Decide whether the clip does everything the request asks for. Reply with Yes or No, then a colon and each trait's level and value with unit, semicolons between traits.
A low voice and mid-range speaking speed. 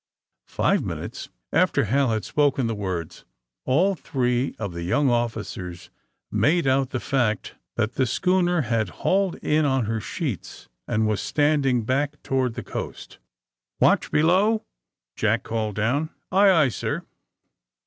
Yes: low, 130 Hz; average, 150 wpm